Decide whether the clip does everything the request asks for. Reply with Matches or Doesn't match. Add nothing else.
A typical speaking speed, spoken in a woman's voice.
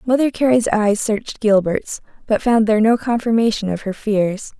Matches